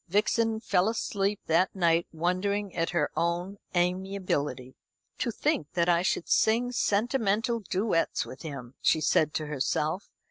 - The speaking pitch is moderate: Yes, medium, 180 Hz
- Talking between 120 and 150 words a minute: Yes, average, 140 wpm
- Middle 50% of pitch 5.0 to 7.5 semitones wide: No, average, 3.8 semitones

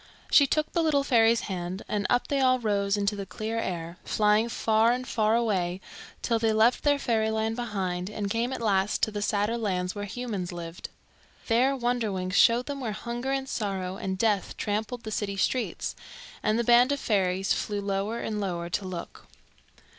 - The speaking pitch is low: No, high, 215 Hz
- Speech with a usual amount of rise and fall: Yes, average, 3.4 semitones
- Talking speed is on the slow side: No, average, 185 wpm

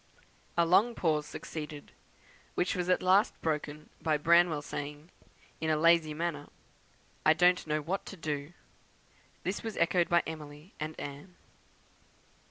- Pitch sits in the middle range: Yes, medium, 160 Hz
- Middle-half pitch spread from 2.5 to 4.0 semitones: Yes, average, 2.8 semitones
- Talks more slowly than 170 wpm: Yes, average, 140 wpm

